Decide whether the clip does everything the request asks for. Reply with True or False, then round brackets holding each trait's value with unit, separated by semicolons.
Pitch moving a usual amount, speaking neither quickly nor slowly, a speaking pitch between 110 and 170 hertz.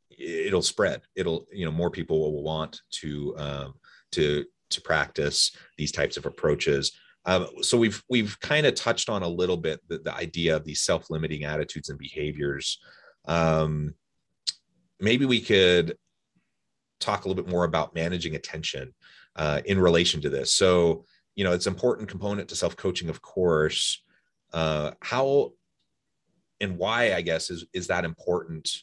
False (3.8 semitones; 160 wpm; 85 Hz)